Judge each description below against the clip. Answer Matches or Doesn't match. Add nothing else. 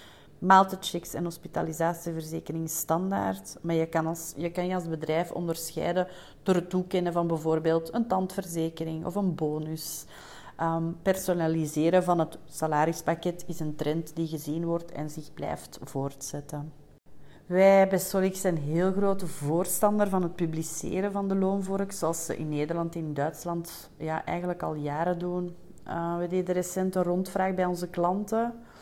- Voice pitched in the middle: Matches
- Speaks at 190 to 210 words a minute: Doesn't match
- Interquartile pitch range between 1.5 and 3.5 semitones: Matches